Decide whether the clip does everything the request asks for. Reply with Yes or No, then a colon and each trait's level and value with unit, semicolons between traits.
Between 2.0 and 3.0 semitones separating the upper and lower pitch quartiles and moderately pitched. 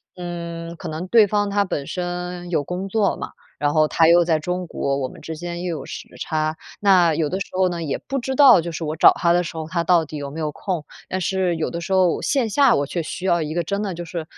Yes: narrow, 2.6 semitones; medium, 175 Hz